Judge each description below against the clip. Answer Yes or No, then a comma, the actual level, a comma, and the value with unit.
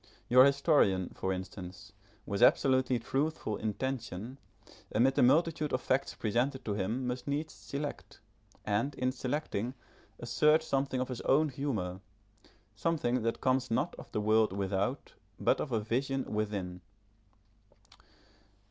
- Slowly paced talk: Yes, slow, 130 wpm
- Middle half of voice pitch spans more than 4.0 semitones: Yes, average, 4.4 semitones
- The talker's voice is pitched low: Yes, low, 125 Hz